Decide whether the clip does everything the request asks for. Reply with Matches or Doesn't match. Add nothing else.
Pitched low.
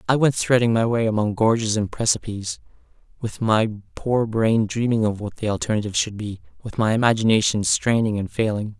Matches